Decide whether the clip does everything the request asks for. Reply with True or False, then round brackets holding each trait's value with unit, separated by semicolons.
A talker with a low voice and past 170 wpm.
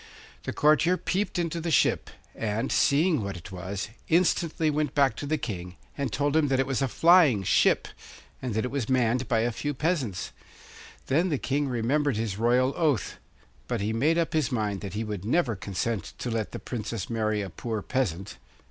True (125 Hz; 195 wpm)